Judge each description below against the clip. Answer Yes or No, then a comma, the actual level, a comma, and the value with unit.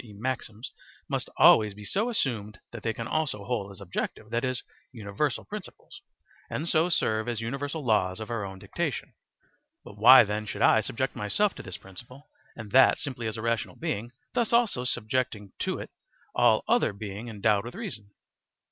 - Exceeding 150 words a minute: Yes, average, 180 wpm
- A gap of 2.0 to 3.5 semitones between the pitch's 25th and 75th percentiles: No, average, 4.0 semitones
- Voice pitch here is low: Yes, low, 115 Hz